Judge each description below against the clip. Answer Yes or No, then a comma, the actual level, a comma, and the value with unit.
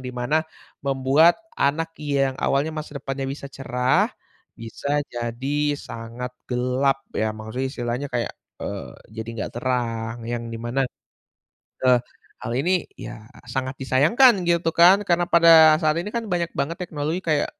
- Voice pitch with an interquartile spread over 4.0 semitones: Yes, average, 4.5 semitones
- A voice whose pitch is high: No, low, 135 Hz